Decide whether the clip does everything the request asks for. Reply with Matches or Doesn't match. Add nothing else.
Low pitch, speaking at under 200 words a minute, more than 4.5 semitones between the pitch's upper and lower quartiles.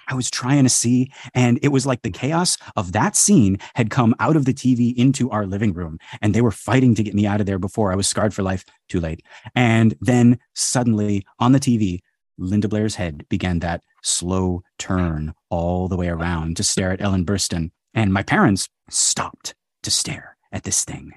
Doesn't match